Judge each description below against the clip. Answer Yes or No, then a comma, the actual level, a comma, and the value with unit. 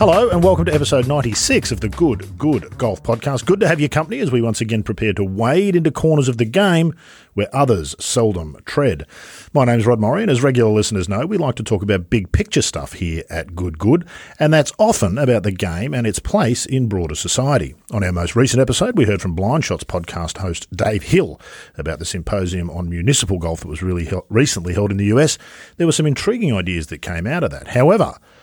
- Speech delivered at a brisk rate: Yes, fast, 225 wpm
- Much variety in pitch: Yes, wide, 7.3 semitones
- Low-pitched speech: Yes, low, 110 Hz